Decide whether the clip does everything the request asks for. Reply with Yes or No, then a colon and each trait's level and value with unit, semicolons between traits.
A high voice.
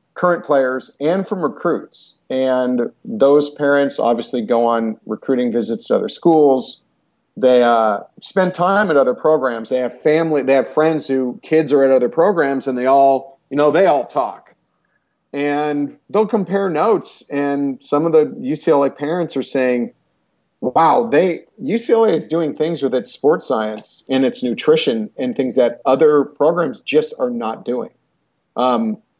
No: medium, 140 Hz